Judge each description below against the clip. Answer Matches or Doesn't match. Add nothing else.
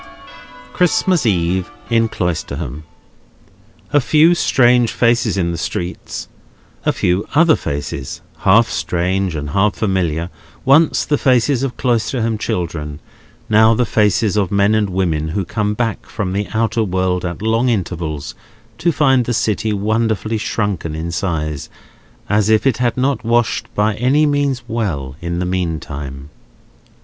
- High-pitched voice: Doesn't match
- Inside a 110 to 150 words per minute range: Matches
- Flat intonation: Doesn't match